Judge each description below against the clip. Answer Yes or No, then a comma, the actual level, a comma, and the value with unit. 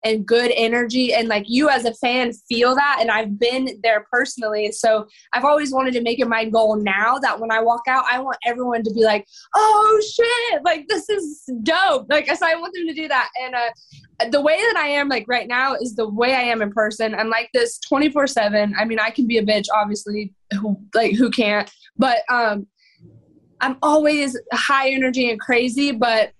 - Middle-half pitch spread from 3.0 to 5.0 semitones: Yes, average, 4.3 semitones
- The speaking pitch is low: No, high, 245 Hz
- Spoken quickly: Yes, fast, 215 wpm